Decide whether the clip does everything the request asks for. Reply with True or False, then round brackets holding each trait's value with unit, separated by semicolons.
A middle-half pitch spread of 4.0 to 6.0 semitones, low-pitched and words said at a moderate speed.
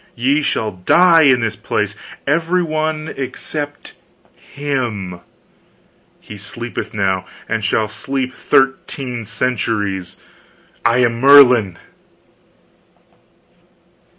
False (5.2 semitones; 125 Hz; 95 wpm)